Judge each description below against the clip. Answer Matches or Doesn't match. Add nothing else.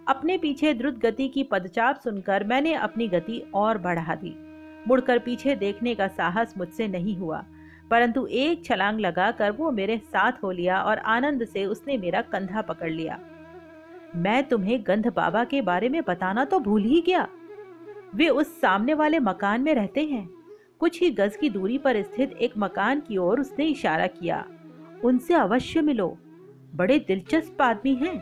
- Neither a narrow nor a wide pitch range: Doesn't match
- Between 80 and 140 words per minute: Doesn't match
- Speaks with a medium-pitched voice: Doesn't match